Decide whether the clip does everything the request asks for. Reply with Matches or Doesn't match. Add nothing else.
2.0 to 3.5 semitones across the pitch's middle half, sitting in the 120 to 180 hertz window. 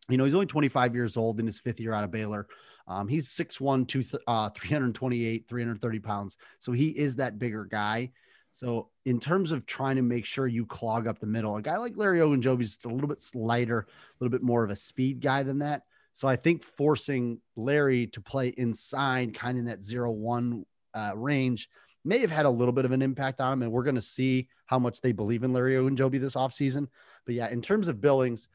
Matches